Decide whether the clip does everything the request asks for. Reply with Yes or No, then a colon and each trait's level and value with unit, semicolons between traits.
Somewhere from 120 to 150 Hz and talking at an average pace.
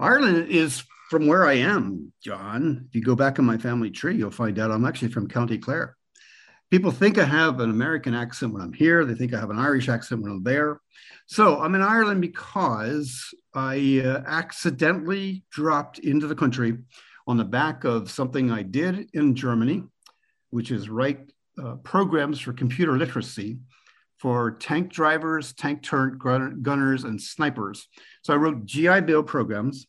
Yes: low, 135 Hz; average, 175 wpm